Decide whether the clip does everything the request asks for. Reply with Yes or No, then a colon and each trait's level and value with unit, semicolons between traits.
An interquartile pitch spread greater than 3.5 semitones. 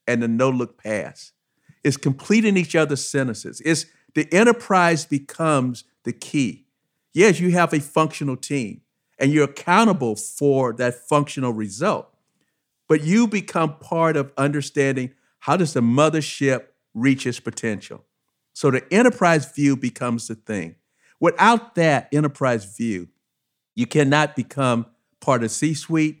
Yes: average, 4.4 semitones